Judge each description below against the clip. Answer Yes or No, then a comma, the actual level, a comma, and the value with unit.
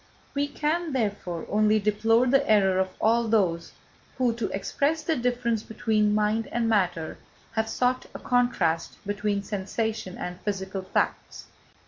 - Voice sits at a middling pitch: No, high, 215 Hz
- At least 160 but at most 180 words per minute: No, average, 140 wpm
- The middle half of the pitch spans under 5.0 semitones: Yes, average, 3.6 semitones